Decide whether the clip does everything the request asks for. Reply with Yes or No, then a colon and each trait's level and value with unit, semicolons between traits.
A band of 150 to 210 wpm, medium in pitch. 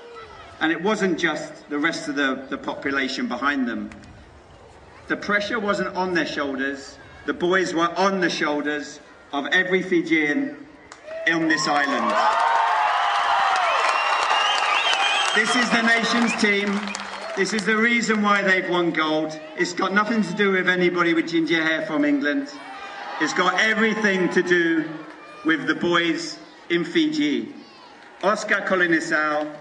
No: slow, 135 wpm; medium, 175 Hz